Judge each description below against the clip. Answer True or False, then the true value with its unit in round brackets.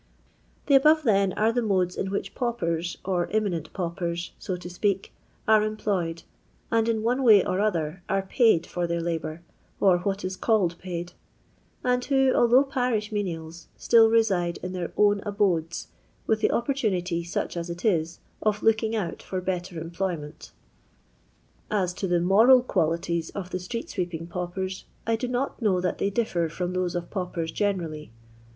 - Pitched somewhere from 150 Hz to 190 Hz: True (185 Hz)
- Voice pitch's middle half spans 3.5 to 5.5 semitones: True (4.1 semitones)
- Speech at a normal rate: True (165 wpm)